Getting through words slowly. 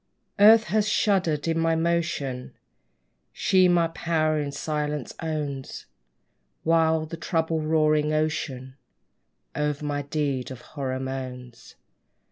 Yes: slow, 110 wpm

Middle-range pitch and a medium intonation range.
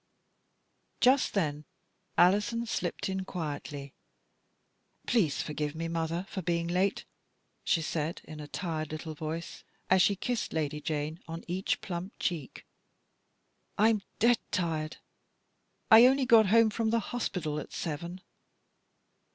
Yes: medium, 170 Hz; average, 4.9 semitones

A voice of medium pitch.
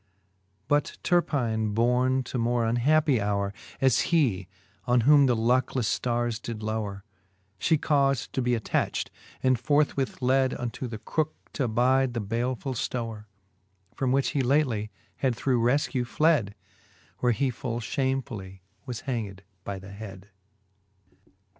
No: low, 125 Hz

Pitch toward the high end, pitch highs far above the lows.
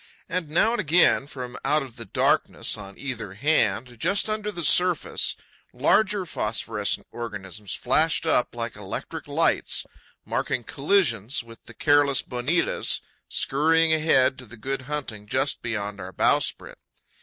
No: low, 135 Hz; wide, 6.2 semitones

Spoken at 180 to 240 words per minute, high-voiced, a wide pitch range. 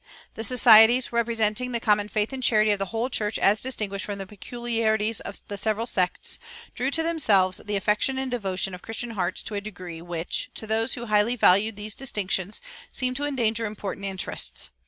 No: average, 195 wpm; high, 215 Hz; average, 3.0 semitones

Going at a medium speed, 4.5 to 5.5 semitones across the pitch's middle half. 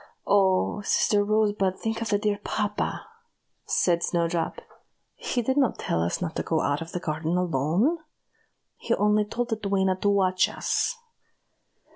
No: average, 155 wpm; average, 3.7 semitones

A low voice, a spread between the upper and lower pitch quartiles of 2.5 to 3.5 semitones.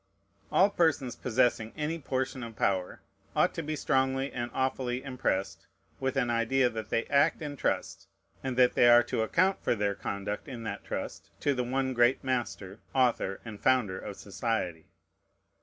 Yes: low, 125 Hz; average, 3.1 semitones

